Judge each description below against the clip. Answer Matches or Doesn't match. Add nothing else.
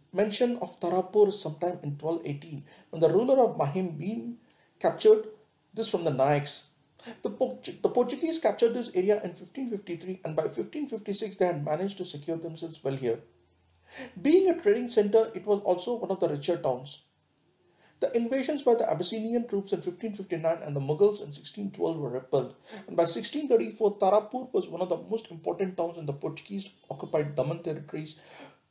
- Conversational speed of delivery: Matches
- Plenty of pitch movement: Matches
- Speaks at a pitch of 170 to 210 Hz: Matches